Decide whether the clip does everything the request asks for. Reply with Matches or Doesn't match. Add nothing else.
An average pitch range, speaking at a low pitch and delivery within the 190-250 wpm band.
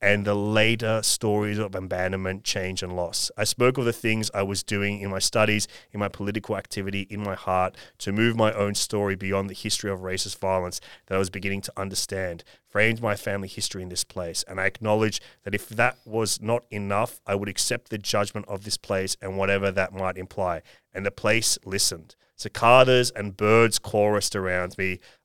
Doesn't match